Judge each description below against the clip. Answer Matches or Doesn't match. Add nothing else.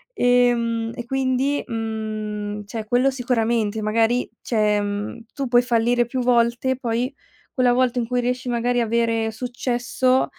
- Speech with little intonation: Matches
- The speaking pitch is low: Doesn't match